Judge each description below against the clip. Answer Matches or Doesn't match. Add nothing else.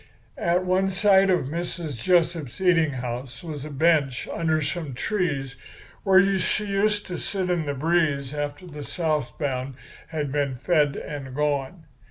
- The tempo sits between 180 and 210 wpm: Doesn't match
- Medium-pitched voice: Matches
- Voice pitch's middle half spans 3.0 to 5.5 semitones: Matches